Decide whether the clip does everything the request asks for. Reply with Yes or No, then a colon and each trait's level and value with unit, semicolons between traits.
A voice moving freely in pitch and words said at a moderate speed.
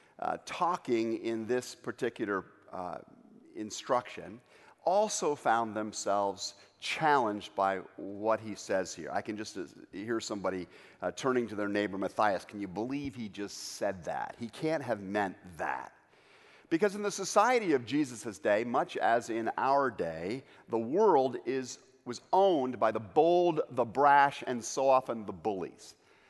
Yes: wide, 6.0 semitones; average, 155 wpm